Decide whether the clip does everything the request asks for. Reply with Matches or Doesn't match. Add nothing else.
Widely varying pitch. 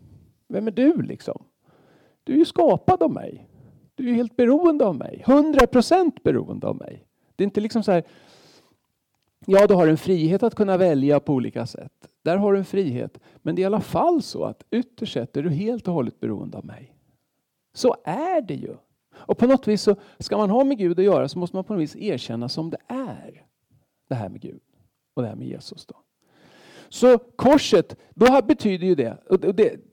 Matches